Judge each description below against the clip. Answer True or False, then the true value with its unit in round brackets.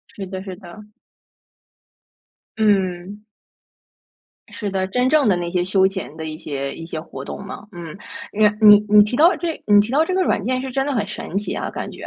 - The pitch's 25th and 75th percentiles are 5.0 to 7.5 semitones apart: False (3.8 semitones)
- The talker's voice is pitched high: True (205 Hz)